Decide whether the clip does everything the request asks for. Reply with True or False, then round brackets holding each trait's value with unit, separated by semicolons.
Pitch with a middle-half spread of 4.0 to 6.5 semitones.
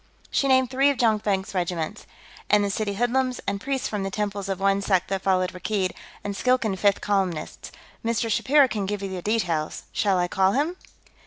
False (3.4 semitones)